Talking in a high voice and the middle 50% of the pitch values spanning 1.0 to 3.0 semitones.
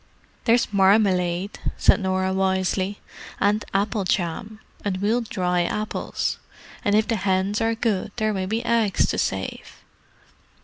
Yes: high, 200 Hz; narrow, 2.4 semitones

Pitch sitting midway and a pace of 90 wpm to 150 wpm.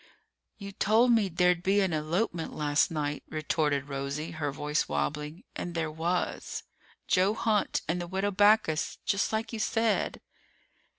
Yes: medium, 175 Hz; average, 145 wpm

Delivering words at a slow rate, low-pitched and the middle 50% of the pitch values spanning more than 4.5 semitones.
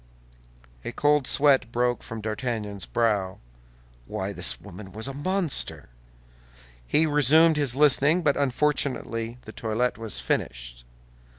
Yes: slow, 120 wpm; low, 120 Hz; average, 5.3 semitones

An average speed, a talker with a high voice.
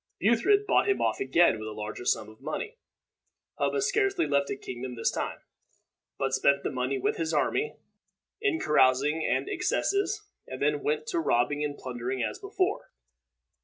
No: average, 165 wpm; medium, 150 Hz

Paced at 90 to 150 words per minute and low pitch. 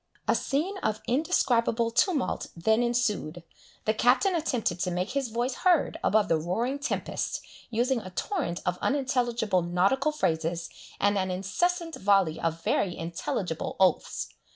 No: average, 140 wpm; high, 225 Hz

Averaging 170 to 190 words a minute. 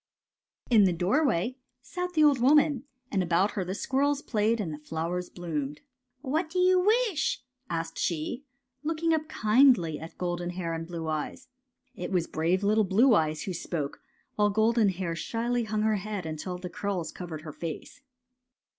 Yes: average, 180 wpm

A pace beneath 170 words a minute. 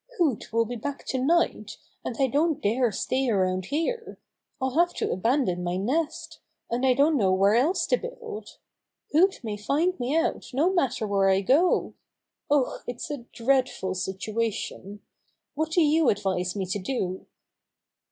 Yes: average, 160 wpm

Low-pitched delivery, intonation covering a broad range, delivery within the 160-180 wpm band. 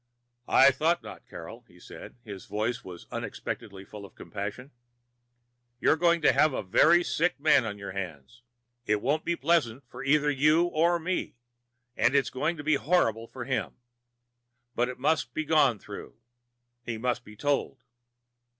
Yes: low, 130 Hz; wide, 6.4 semitones; average, 170 wpm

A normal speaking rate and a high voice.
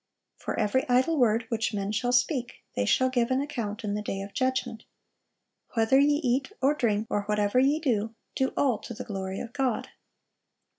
Yes: average, 190 wpm; high, 240 Hz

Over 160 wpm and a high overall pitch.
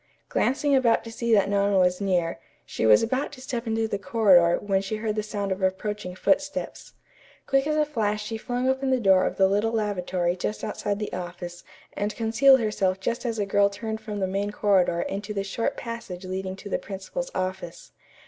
Yes: fast, 205 wpm; high, 205 Hz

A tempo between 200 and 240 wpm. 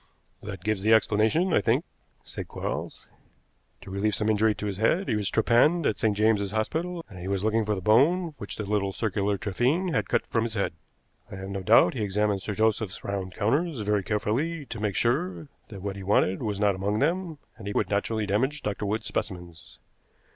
Yes: fast, 205 wpm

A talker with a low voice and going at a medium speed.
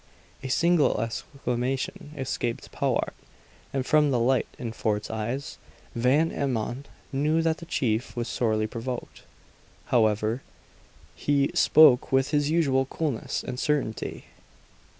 No: low, 130 Hz; slow, 120 wpm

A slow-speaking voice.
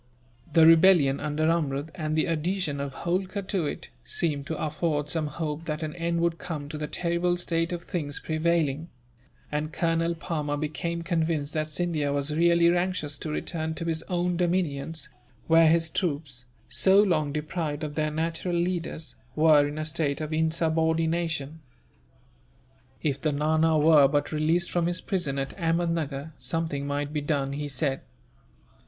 No: average, 160 wpm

